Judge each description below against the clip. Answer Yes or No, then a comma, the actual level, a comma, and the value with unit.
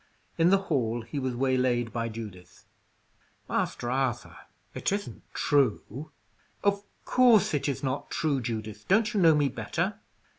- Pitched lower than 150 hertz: Yes, low, 135 Hz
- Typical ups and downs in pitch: No, wide, 6.1 semitones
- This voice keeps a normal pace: Yes, average, 145 wpm